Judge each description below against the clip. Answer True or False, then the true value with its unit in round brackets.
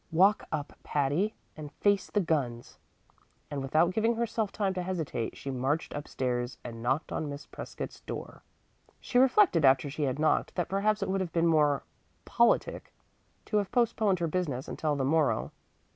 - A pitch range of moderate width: False (6.0 semitones)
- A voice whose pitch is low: False (160 Hz)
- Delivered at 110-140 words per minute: False (175 wpm)